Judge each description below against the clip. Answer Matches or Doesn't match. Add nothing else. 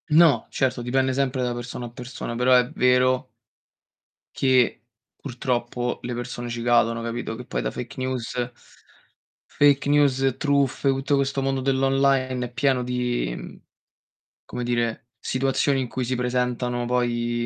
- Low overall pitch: Matches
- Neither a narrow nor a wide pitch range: Doesn't match